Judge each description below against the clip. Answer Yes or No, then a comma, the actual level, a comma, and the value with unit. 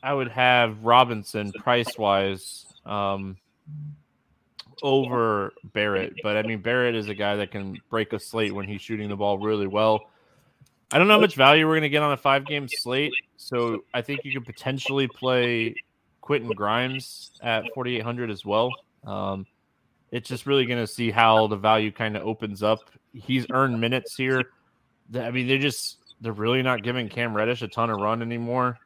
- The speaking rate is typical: Yes, average, 185 wpm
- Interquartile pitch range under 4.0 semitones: Yes, average, 3.2 semitones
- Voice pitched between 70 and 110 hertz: No, low, 120 Hz